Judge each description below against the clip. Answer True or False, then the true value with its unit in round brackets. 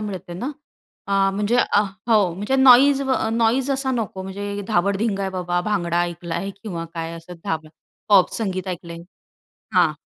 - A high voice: True (195 Hz)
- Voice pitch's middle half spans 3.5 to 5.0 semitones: True (4.1 semitones)